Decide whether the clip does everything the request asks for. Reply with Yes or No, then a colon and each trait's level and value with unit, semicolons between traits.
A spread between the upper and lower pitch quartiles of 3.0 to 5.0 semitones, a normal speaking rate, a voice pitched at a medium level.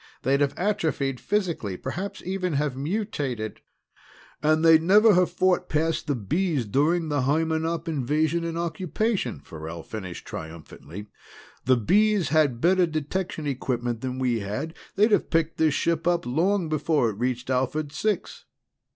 No: wide, 5.4 semitones; average, 150 wpm; medium, 155 Hz